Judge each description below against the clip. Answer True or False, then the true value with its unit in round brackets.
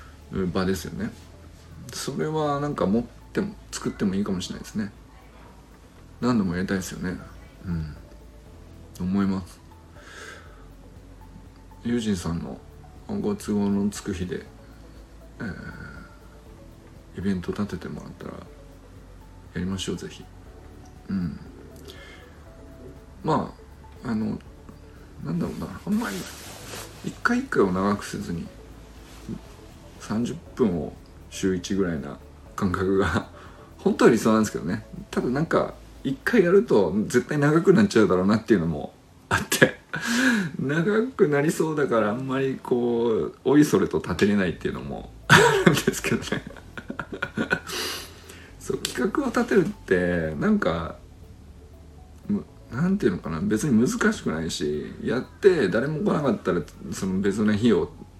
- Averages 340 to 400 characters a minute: False (255 characters per minute)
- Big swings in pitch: True (6.4 semitones)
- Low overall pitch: True (95 Hz)